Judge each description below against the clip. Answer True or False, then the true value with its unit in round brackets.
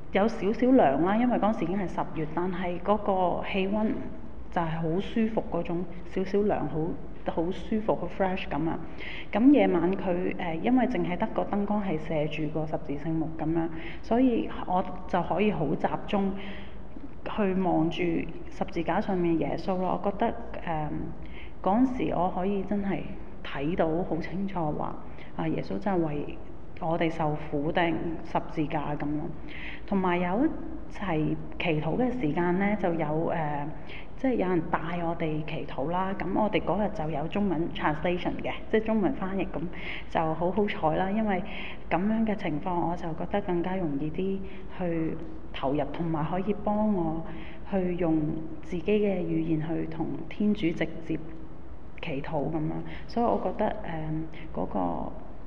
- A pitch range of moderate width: True (3.6 semitones)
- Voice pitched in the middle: True (175 Hz)